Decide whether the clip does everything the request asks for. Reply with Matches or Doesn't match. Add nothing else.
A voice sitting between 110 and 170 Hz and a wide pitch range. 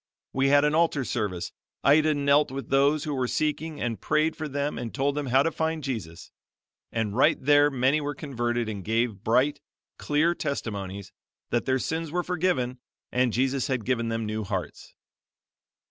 Doesn't match